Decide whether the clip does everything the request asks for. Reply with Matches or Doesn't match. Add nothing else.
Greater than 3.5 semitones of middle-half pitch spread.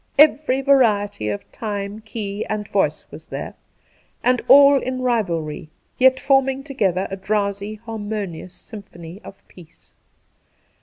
Matches